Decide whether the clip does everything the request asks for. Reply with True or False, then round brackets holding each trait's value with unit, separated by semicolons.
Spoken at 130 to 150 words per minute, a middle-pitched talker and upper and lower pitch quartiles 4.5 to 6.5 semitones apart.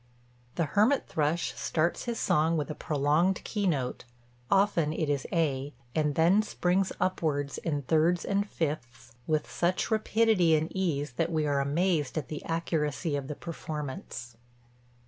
False (145 wpm; 160 Hz; 3.4 semitones)